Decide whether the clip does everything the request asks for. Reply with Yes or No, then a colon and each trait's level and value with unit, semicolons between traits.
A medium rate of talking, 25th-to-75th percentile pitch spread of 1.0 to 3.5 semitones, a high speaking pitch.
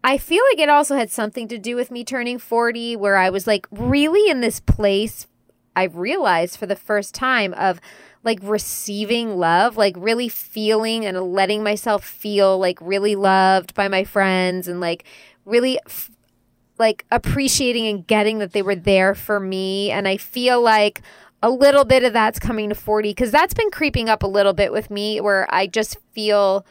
Yes: average, 190 wpm; average, 3.1 semitones; high, 210 Hz